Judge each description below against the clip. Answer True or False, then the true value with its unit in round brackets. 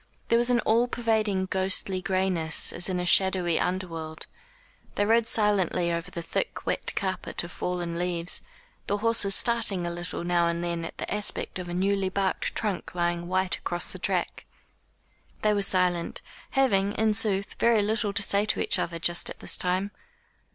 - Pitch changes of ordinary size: True (3.0 semitones)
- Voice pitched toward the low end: False (190 Hz)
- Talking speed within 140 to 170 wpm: False (180 wpm)